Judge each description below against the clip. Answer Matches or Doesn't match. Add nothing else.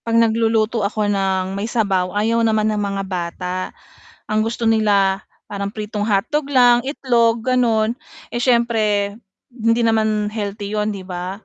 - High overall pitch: Matches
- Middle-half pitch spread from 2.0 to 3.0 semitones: Matches